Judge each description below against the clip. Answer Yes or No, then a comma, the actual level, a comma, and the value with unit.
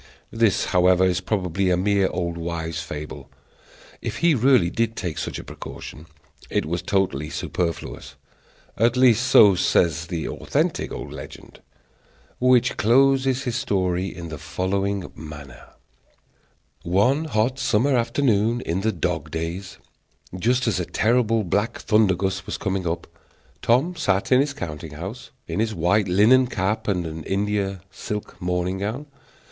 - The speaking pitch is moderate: No, very low, 95 Hz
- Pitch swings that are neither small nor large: Yes, average, 4.8 semitones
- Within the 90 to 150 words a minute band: Yes, average, 145 wpm